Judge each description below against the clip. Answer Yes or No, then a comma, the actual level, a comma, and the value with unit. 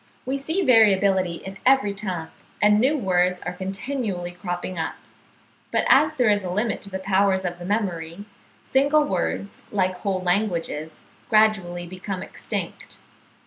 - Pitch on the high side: Yes, high, 195 Hz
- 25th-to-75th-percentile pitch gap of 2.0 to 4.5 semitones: Yes, average, 3.2 semitones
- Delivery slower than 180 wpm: Yes, average, 145 wpm